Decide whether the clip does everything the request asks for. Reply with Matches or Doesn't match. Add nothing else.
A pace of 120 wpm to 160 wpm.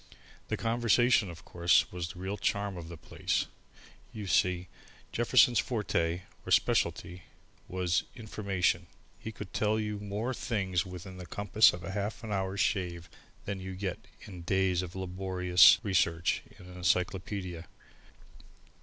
Matches